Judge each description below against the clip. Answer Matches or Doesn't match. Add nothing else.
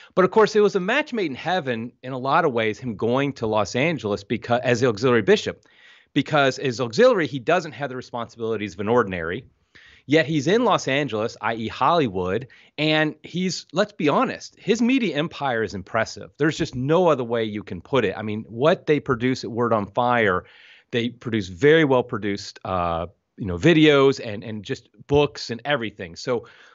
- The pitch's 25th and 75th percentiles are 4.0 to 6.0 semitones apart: Matches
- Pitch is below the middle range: Matches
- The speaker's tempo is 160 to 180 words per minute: Doesn't match